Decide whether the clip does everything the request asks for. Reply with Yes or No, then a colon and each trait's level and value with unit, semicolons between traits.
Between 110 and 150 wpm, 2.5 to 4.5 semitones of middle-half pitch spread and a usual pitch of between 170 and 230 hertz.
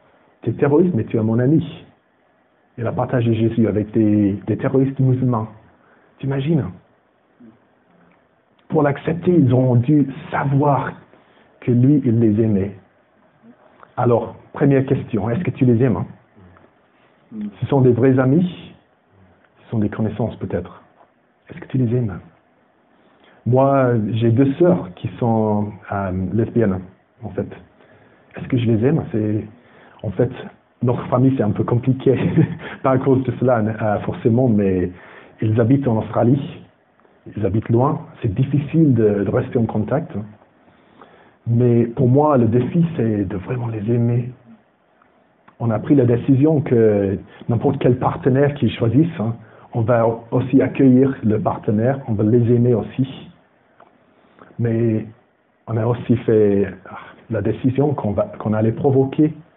No: average, 140 wpm; average, 3.6 semitones; low, 120 Hz